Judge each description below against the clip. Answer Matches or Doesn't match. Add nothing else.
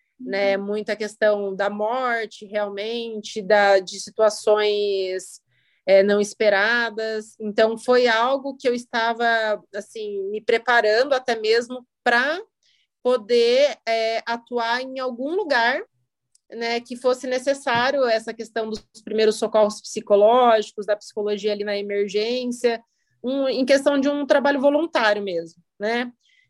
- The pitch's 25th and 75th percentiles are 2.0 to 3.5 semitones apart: Matches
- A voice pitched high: Matches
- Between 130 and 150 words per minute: Doesn't match